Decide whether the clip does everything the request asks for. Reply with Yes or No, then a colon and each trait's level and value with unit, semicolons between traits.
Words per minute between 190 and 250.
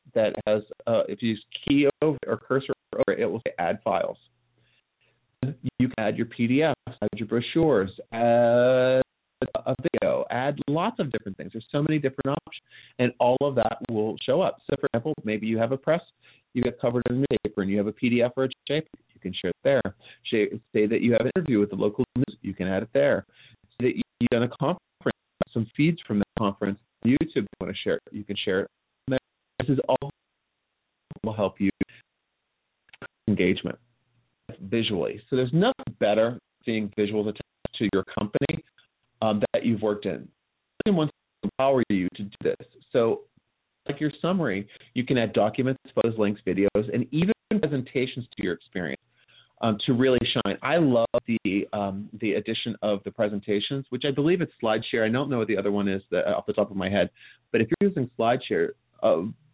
Yes: average, 200 wpm